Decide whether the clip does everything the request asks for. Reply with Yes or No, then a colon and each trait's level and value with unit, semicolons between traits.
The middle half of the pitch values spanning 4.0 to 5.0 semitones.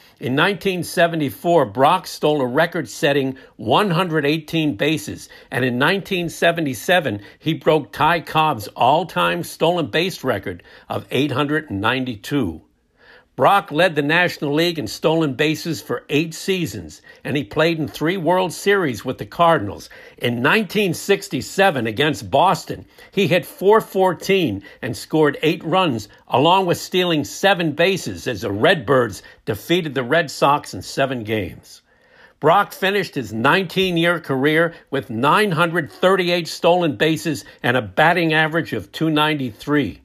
Yes: average, 4.3 semitones